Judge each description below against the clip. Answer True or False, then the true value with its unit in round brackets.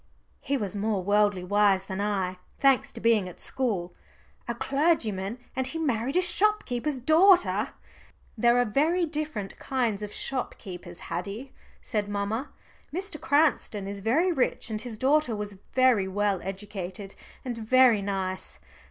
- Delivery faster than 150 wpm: False (145 wpm)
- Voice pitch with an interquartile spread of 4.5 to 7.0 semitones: True (5.2 semitones)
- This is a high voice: True (220 Hz)